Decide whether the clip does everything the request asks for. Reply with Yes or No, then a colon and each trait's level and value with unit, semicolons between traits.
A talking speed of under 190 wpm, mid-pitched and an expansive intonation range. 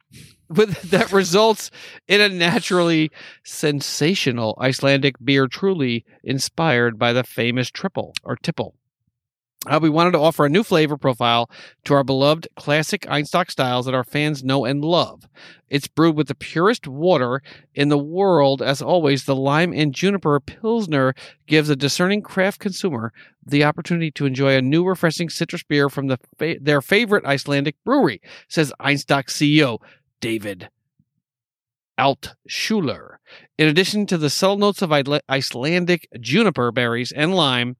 No: average, 150 wpm; medium, 145 Hz; average, 4.5 semitones